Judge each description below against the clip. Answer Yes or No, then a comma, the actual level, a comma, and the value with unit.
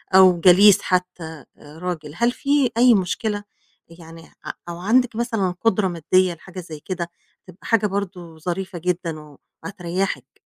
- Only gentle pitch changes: No, average, 3.3 semitones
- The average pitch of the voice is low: No, medium, 180 Hz